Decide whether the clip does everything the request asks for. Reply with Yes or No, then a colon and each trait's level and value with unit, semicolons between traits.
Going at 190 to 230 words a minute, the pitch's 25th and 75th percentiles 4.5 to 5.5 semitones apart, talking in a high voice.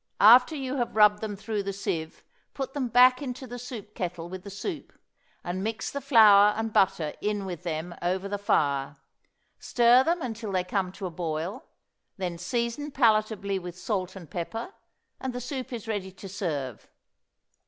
No: average, 175 wpm; average, 4.9 semitones; high, 205 Hz